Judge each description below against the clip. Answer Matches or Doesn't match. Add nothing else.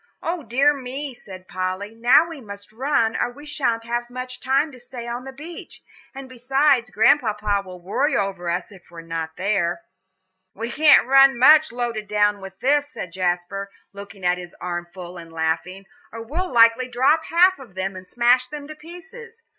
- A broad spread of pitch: Matches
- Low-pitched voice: Doesn't match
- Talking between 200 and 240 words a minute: Doesn't match